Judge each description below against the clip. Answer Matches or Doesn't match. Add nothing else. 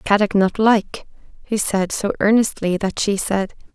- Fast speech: Doesn't match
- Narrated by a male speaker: Doesn't match